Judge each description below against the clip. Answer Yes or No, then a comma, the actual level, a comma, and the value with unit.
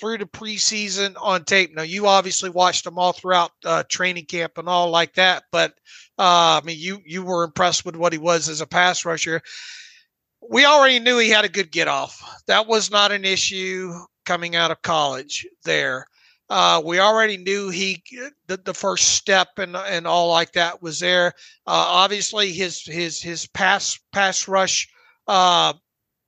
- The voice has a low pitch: No, medium, 185 Hz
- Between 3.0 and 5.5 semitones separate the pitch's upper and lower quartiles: No, narrow, 2.6 semitones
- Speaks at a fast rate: No, average, 180 wpm